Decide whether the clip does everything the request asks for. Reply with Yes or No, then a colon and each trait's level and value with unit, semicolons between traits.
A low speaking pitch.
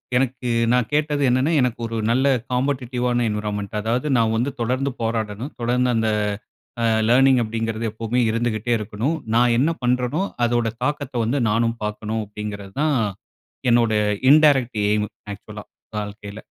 Yes: low, 120 Hz